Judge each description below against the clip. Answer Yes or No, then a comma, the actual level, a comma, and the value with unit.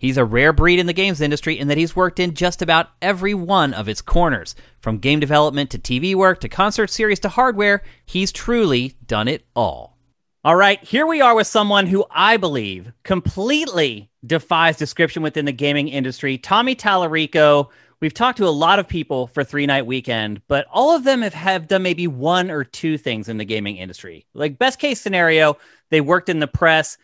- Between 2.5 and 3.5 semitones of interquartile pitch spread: No, wide, 5.6 semitones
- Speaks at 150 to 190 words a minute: No, average, 200 wpm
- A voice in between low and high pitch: Yes, medium, 165 Hz